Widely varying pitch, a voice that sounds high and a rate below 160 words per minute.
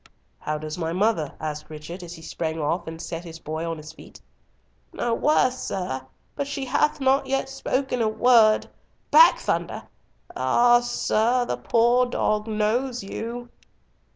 Yes: wide, 7.2 semitones; high, 215 Hz; average, 150 wpm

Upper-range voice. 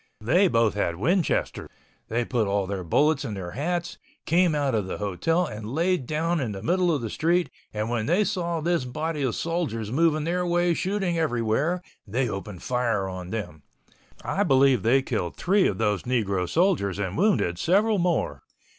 No: low, 135 Hz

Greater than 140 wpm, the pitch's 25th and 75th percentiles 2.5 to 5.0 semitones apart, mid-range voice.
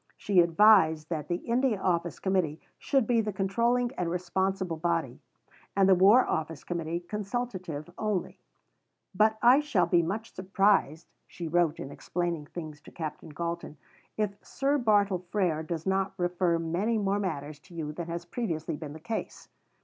Yes: average, 160 wpm; average, 4.0 semitones; medium, 180 Hz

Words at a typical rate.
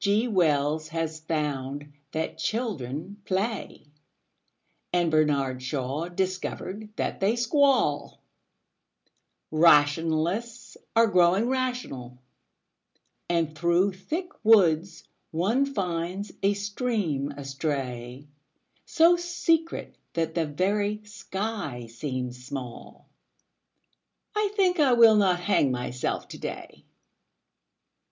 No: slow, 95 wpm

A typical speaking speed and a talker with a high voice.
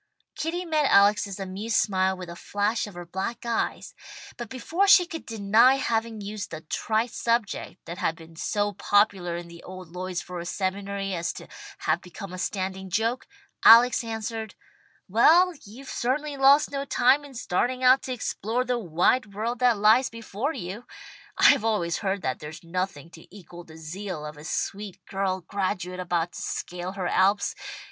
Yes: average, 170 wpm; high, 200 Hz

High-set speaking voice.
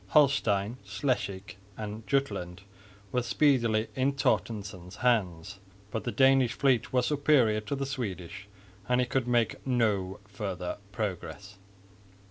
No: low, 115 Hz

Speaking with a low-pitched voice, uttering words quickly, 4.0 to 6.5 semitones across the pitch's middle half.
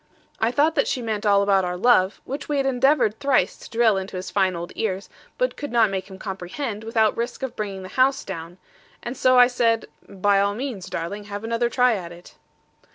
No: high, 215 Hz; fast, 220 wpm; average, 4.5 semitones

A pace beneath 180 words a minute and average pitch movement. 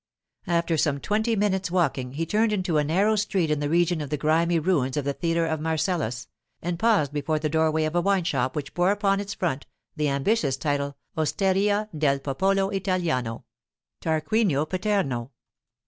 Yes: average, 170 wpm; average, 4.7 semitones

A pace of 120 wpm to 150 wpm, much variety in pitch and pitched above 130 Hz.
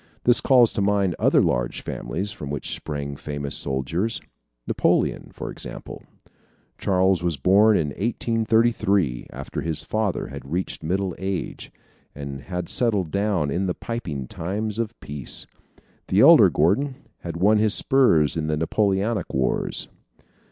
No: average, 140 wpm; wide, 6.1 semitones; very low, 95 Hz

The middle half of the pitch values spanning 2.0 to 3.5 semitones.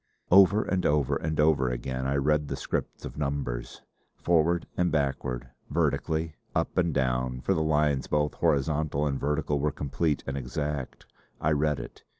Yes: narrow, 2.5 semitones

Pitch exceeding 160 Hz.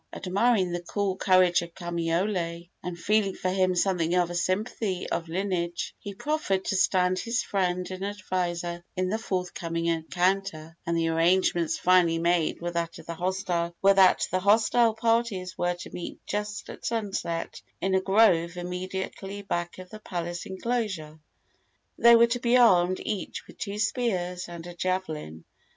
Yes: medium, 185 Hz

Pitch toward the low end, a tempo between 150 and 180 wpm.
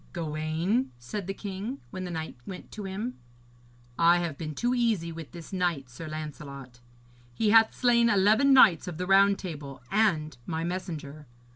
No: medium, 175 Hz; average, 165 wpm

